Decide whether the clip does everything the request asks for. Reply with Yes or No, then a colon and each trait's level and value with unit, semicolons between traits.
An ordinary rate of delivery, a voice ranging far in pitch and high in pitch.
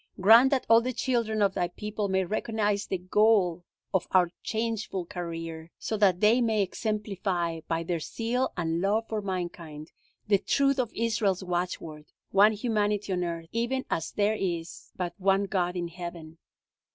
No: average, 165 wpm; average, 3.8 semitones; high, 195 Hz